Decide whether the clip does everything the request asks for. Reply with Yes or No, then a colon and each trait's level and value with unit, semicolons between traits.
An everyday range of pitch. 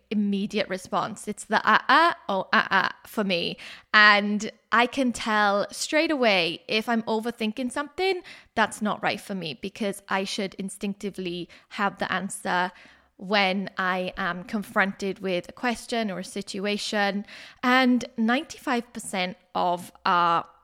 Yes: average, 3.2 semitones